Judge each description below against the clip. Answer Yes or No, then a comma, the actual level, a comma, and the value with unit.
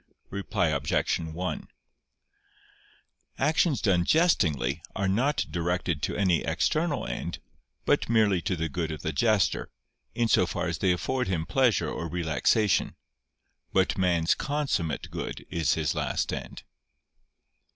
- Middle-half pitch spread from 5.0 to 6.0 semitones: Yes, wide, 5.4 semitones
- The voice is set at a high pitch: No, very low, 90 Hz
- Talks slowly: Yes, slow, 130 wpm